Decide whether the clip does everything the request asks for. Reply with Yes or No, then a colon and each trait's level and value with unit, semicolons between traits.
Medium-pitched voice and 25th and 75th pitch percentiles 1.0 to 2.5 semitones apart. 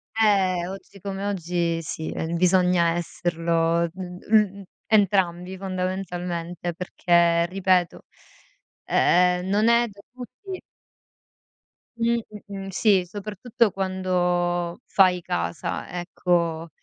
Yes: medium, 180 Hz; narrow, 2.2 semitones